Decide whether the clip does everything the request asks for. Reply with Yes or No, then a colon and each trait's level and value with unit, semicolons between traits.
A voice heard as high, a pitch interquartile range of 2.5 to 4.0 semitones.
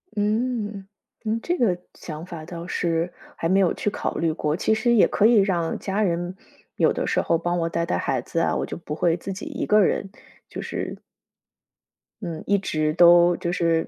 No: medium, 175 Hz; average, 3.6 semitones